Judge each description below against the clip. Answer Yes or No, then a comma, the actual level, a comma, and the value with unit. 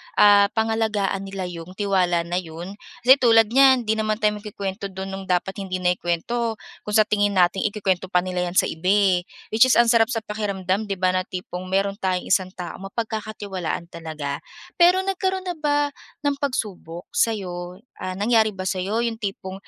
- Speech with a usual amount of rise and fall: Yes, average, 3.2 semitones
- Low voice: No, high, 200 Hz